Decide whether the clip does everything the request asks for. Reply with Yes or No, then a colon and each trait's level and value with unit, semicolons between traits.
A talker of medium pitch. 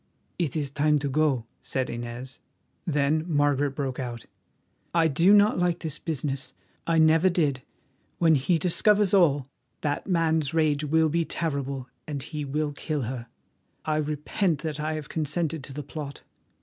Yes: medium, 150 Hz